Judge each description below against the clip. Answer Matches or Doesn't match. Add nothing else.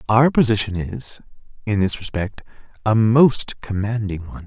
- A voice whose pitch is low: Matches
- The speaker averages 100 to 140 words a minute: Matches